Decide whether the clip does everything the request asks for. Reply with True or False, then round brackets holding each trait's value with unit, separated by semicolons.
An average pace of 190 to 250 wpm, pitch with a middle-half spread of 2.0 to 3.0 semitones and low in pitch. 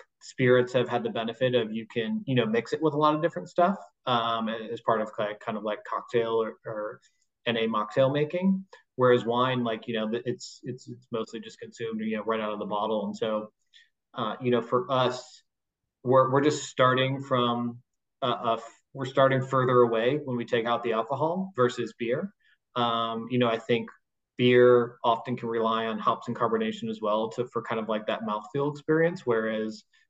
True (200 wpm; 2.7 semitones; 120 Hz)